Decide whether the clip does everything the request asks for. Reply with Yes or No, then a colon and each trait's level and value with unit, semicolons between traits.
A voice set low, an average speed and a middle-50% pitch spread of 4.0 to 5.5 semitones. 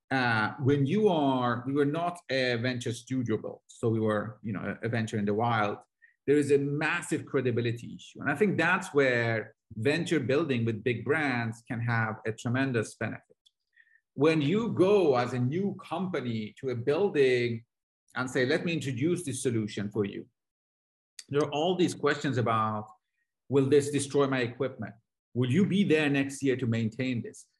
Yes: low, 130 Hz; average, 175 wpm; average, 4.4 semitones